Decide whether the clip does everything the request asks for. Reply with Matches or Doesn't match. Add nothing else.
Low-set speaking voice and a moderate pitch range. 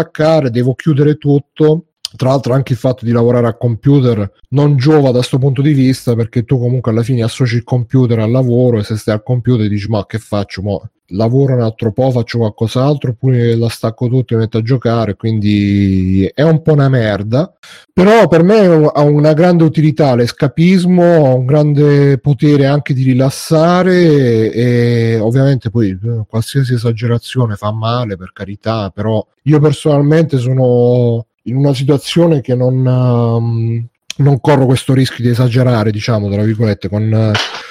Matches